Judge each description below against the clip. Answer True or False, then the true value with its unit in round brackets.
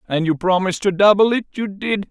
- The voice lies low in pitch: False (195 Hz)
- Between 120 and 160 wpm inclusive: False (200 wpm)